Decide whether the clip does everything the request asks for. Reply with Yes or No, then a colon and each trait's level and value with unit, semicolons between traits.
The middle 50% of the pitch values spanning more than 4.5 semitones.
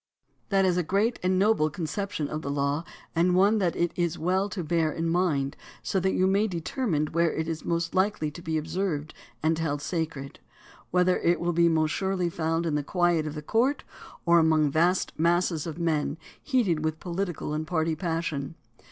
No: average, 2.7 semitones